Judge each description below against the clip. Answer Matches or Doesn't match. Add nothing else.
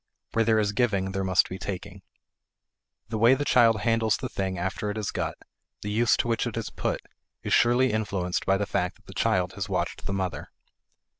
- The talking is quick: Matches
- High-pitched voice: Doesn't match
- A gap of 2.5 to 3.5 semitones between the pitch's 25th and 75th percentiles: Matches